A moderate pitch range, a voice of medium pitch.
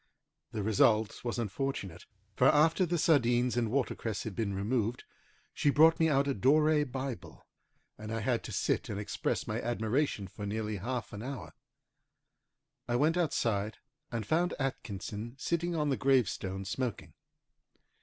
No: average, 5.0 semitones; low, 120 Hz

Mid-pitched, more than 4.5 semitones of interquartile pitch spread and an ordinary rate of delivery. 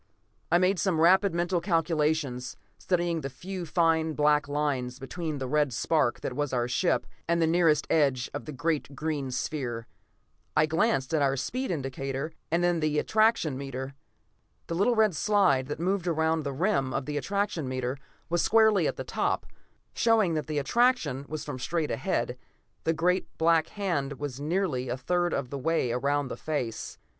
No: medium, 155 Hz; average, 4.2 semitones; average, 175 wpm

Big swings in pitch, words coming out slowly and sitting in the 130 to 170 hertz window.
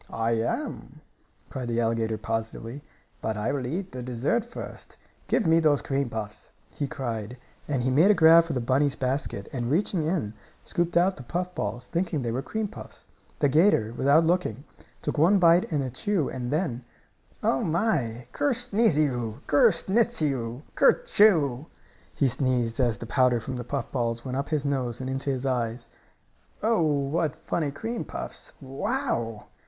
No: wide, 5.7 semitones; average, 170 wpm; low, 135 Hz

